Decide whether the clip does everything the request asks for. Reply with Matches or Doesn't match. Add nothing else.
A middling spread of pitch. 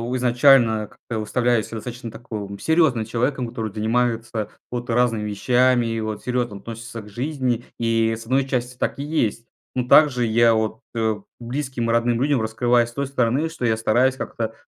Doesn't match